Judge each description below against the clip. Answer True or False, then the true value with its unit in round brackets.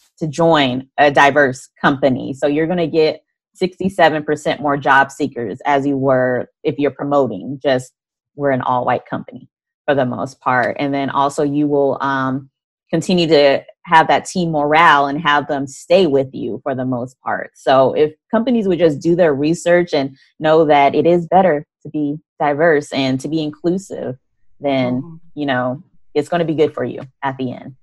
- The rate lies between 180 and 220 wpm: True (185 wpm)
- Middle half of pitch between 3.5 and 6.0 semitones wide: False (2.9 semitones)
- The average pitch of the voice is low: False (145 Hz)